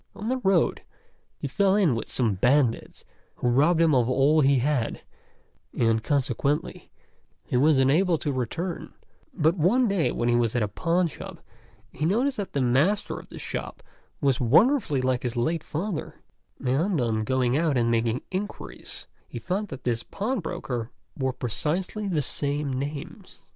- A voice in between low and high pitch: Yes, medium, 145 Hz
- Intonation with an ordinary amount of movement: No, wide, 6.3 semitones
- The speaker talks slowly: No, average, 160 wpm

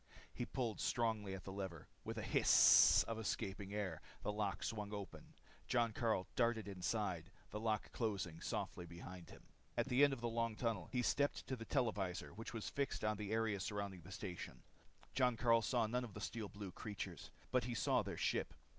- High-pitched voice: No, low, 110 Hz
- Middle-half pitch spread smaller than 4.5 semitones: Yes, average, 3.1 semitones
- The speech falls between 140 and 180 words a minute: No, average, 190 wpm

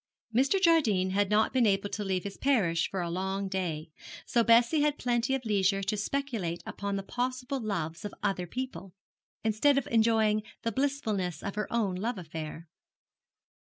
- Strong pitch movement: No, average, 4.5 semitones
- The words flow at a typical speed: Yes, average, 170 wpm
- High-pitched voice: Yes, high, 210 Hz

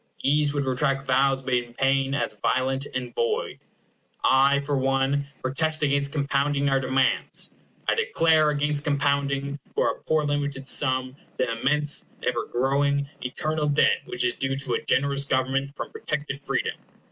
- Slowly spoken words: No, average, 150 wpm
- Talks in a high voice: No, medium, 140 Hz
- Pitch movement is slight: Yes, narrow, 1.5 semitones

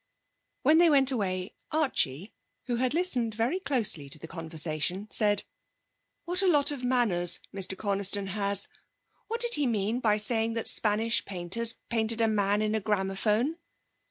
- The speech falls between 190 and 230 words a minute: No, average, 155 wpm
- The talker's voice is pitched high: Yes, high, 220 Hz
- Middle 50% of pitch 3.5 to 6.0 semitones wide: Yes, average, 4.6 semitones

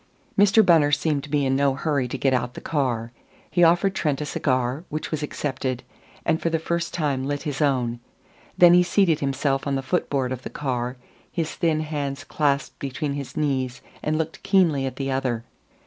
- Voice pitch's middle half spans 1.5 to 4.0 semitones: Yes, average, 3.2 semitones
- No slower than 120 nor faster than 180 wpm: No, average, 200 wpm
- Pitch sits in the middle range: Yes, medium, 145 Hz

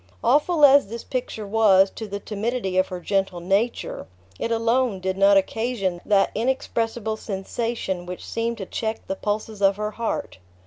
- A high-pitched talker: Yes, high, 215 Hz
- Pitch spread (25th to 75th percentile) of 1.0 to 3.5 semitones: Yes, average, 3.2 semitones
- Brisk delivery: No, average, 165 wpm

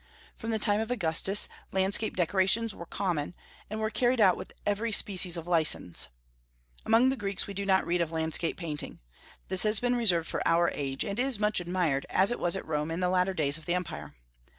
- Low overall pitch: No, medium, 185 Hz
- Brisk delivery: Yes, fast, 210 wpm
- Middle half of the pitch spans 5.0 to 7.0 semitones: No, average, 4.1 semitones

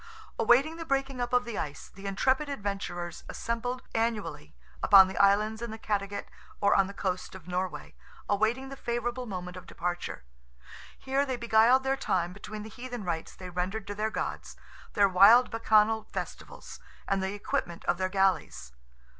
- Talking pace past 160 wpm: Yes, average, 170 wpm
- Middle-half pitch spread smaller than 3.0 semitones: No, average, 4.2 semitones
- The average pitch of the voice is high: Yes, high, 210 Hz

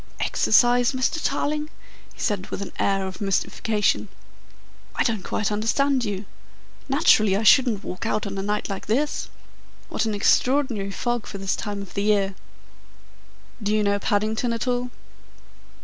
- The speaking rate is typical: Yes, average, 155 wpm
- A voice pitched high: Yes, high, 215 Hz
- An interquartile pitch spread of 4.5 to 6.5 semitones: No, average, 3.5 semitones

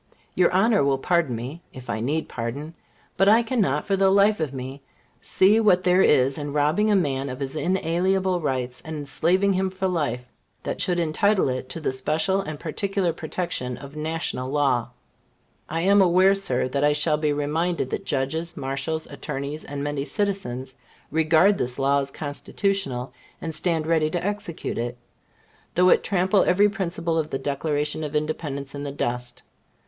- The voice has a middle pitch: Yes, medium, 155 Hz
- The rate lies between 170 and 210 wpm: Yes, average, 175 wpm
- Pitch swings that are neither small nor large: Yes, average, 5.0 semitones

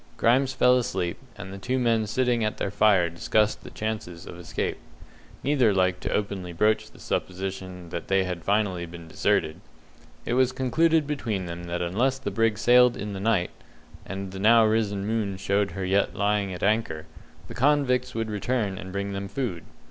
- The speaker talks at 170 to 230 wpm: Yes, average, 185 wpm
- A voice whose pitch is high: No, low, 100 Hz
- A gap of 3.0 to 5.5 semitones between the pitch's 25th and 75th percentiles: Yes, average, 4.0 semitones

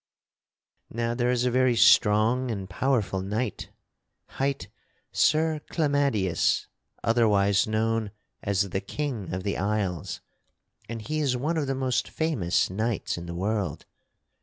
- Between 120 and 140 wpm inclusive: Yes, slow, 135 wpm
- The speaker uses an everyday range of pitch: Yes, average, 4.5 semitones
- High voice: No, low, 115 Hz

